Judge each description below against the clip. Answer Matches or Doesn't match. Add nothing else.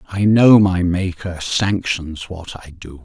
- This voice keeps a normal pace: Matches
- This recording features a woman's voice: Doesn't match